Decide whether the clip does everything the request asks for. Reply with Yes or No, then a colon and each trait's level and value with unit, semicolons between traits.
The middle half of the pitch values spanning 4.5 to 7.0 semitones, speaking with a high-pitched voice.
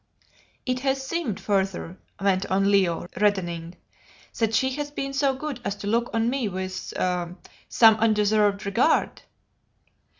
Yes: average, 5.1 semitones; high, 210 Hz